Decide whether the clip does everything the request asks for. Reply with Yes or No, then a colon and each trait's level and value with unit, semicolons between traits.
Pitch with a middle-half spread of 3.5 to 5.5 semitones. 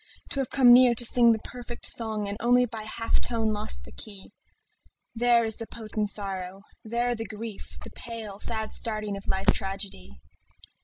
No: narrow, 2.6 semitones